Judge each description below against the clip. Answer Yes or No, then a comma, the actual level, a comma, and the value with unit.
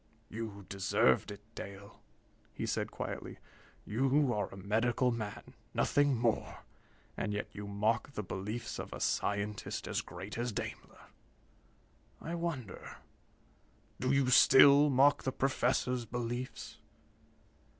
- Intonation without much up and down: No, average, 4.3 semitones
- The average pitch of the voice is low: Yes, low, 115 Hz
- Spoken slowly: Yes, slow, 120 wpm